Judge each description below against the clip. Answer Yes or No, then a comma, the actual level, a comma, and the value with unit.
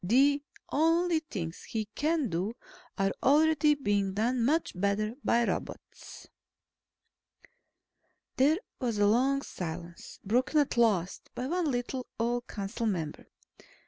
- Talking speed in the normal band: No, slow, 120 wpm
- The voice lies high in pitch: Yes, high, 240 Hz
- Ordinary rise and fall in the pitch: No, wide, 6.1 semitones